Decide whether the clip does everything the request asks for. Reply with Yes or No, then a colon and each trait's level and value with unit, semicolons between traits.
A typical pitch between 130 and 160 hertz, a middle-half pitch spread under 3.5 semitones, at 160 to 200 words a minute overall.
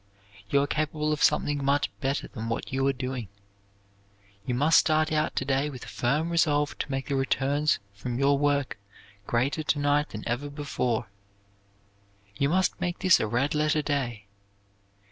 Yes: medium, 140 Hz; average, 2.8 semitones; average, 170 wpm